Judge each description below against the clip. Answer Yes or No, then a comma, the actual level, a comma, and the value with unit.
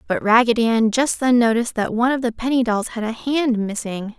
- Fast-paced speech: Yes, fast, 230 wpm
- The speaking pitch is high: Yes, high, 235 Hz